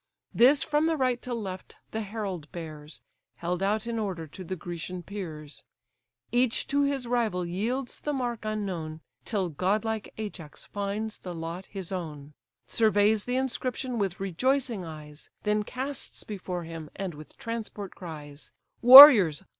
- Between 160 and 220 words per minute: No, average, 145 wpm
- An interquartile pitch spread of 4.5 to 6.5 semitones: Yes, wide, 5.5 semitones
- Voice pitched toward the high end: Yes, high, 200 Hz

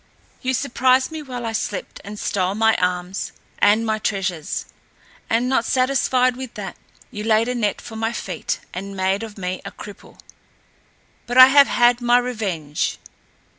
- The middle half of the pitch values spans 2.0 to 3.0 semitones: No, average, 4.0 semitones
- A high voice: Yes, high, 225 Hz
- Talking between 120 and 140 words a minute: No, average, 165 wpm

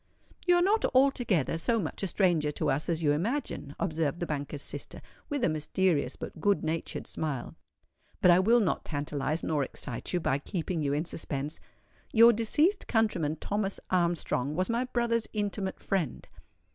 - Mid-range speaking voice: Yes, medium, 175 Hz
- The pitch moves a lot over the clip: Yes, wide, 6.7 semitones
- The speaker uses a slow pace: No, average, 170 wpm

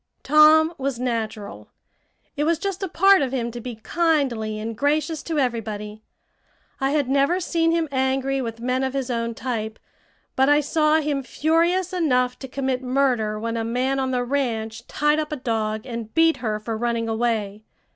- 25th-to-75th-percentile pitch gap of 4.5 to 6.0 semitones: Yes, average, 4.8 semitones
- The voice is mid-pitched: No, very high, 260 Hz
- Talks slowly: No, average, 180 wpm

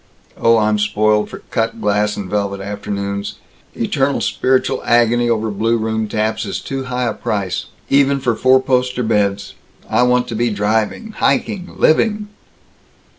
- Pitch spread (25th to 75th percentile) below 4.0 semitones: Yes, average, 3.3 semitones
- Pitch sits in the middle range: No, low, 110 Hz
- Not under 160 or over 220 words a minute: No, average, 150 wpm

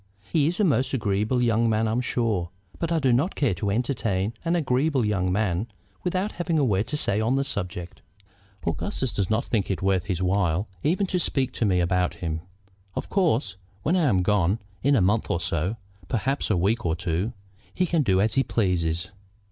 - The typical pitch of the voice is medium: No, low, 110 Hz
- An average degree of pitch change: No, wide, 6.6 semitones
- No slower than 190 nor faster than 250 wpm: Yes, fast, 205 wpm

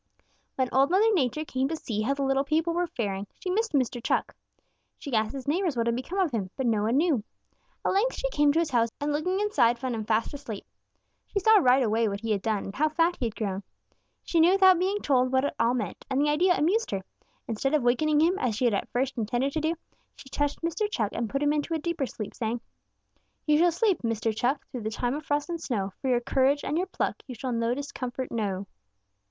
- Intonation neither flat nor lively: No, wide, 5.7 semitones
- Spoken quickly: Yes, fast, 245 wpm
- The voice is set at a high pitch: Yes, very high, 270 Hz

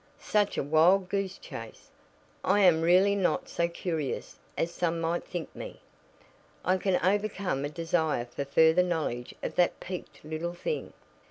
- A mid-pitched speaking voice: Yes, medium, 175 Hz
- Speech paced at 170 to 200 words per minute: No, average, 155 wpm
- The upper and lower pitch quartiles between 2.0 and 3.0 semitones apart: Yes, average, 2.7 semitones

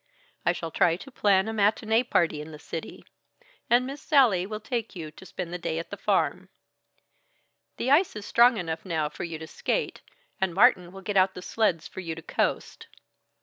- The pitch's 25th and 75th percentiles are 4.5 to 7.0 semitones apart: Yes, average, 4.9 semitones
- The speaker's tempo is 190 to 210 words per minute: Yes, average, 200 wpm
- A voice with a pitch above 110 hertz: Yes, high, 190 Hz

